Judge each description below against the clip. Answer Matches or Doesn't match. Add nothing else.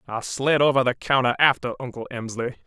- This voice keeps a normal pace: Matches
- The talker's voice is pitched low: Matches